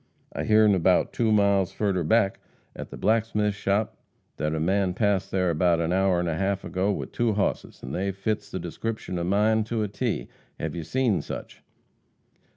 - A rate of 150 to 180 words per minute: No, average, 190 wpm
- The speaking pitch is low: Yes, low, 100 Hz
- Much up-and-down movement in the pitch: No, average, 3.1 semitones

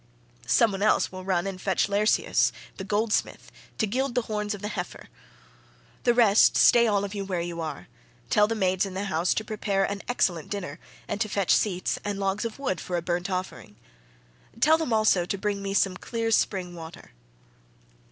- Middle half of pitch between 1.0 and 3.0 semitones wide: Yes, average, 2.7 semitones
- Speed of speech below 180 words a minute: No, average, 195 wpm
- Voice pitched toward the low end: No, high, 200 Hz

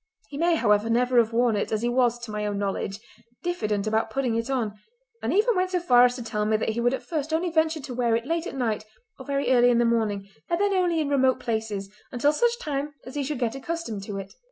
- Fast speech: Yes, fast, 260 wpm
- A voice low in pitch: No, high, 245 Hz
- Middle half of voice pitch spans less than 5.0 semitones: No, wide, 5.5 semitones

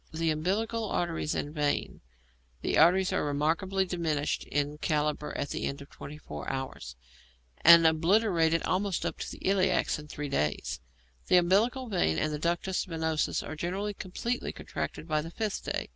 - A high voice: No, medium, 165 Hz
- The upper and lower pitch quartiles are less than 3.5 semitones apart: No, average, 3.9 semitones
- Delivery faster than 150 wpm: Yes, average, 165 wpm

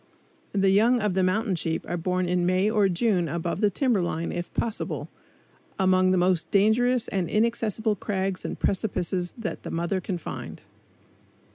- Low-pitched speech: No, high, 190 Hz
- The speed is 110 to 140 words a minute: No, average, 165 wpm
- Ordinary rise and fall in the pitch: Yes, average, 3.3 semitones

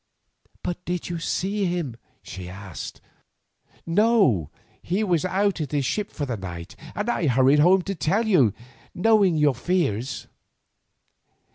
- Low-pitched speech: No, medium, 170 Hz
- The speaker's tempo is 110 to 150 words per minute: Yes, average, 140 wpm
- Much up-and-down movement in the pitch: Yes, wide, 7.1 semitones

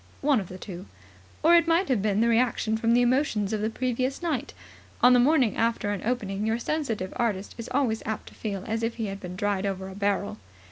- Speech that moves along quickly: Yes, fast, 230 wpm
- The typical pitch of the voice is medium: No, high, 225 Hz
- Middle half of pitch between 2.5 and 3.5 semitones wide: No, average, 3.9 semitones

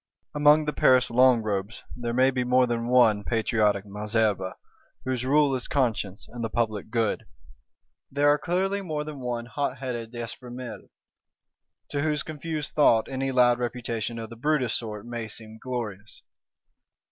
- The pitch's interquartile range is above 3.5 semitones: No, average, 3.2 semitones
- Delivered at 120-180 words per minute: Yes, average, 150 wpm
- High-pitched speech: No, low, 120 Hz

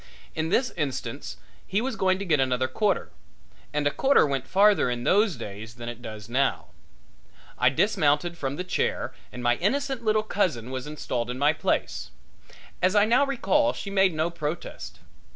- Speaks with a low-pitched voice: No, medium, 155 Hz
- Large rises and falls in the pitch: Yes, wide, 8.0 semitones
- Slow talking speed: No, average, 175 wpm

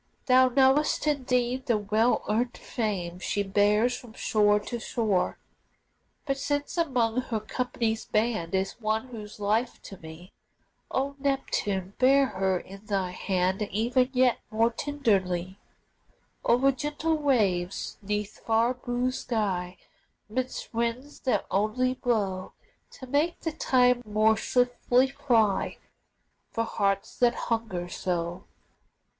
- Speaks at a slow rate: Yes, slow, 125 wpm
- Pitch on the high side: Yes, high, 225 Hz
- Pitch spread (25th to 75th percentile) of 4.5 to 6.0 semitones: No, average, 4.1 semitones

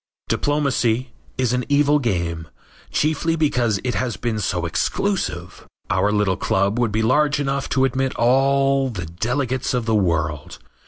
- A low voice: Yes, low, 125 Hz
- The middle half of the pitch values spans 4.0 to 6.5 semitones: Yes, average, 5.2 semitones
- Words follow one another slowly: No, average, 150 wpm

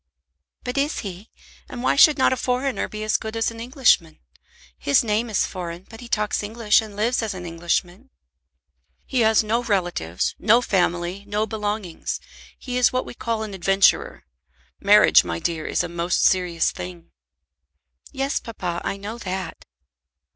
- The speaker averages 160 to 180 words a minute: Yes, average, 165 wpm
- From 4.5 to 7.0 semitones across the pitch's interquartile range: Yes, average, 4.8 semitones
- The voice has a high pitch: Yes, high, 210 Hz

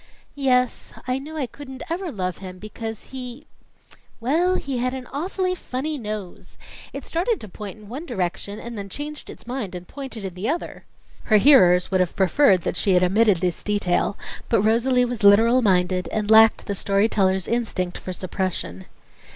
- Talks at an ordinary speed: Yes, average, 180 wpm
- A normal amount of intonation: No, wide, 5.7 semitones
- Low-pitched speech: No, high, 220 Hz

